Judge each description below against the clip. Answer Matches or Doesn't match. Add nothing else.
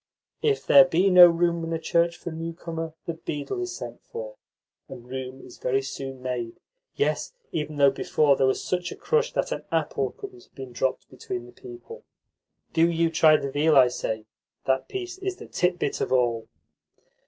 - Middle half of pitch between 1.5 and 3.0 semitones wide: Doesn't match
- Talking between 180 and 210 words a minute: Matches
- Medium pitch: Matches